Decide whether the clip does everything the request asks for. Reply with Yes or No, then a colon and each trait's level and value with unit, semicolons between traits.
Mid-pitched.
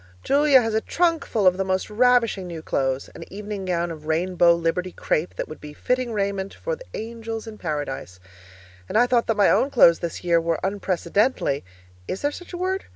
No: high, 195 Hz